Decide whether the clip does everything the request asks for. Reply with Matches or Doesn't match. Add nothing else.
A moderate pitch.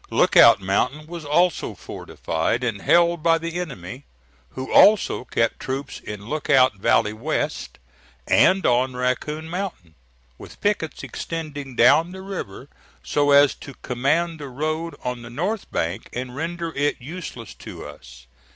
Matches